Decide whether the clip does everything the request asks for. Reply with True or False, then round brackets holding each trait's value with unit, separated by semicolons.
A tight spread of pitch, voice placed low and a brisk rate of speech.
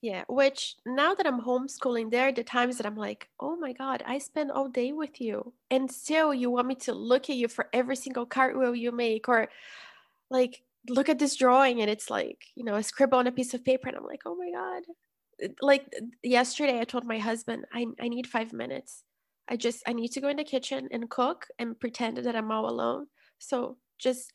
False (2.3 semitones; 255 Hz; 225 wpm)